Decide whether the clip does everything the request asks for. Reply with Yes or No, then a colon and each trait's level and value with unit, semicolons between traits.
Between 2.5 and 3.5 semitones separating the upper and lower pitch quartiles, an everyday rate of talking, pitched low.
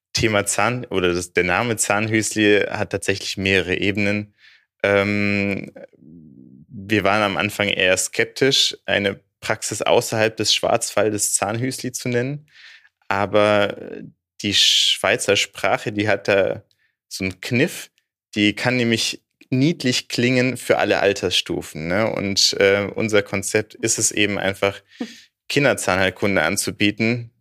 No: average, 2.8 semitones; slow, 120 wpm; low, 105 Hz